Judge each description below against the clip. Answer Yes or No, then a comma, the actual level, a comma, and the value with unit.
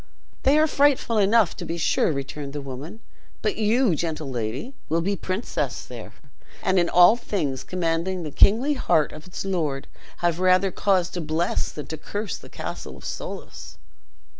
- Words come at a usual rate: Yes, average, 170 wpm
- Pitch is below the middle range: No, medium, 175 Hz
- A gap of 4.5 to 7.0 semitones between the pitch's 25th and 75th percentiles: Yes, average, 5.2 semitones